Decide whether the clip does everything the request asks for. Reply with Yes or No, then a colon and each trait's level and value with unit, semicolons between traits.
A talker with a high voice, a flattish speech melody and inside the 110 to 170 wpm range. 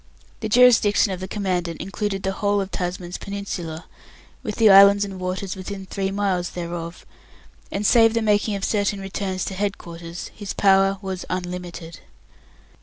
Yes: high, 195 Hz; narrow, 2.0 semitones; average, 160 wpm